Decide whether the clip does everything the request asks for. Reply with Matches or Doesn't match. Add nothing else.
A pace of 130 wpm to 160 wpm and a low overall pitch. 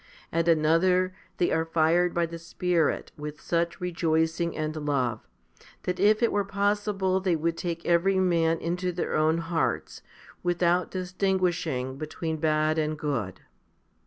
Doesn't match